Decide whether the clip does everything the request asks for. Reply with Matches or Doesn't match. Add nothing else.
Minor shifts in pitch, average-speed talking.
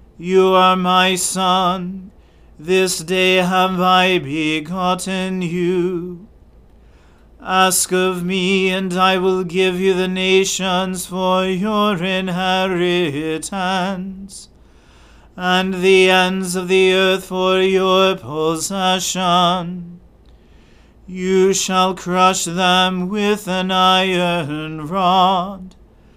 Doesn't match